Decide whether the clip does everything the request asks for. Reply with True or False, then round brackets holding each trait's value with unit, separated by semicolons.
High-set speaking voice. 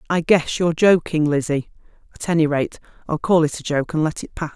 False (160 Hz)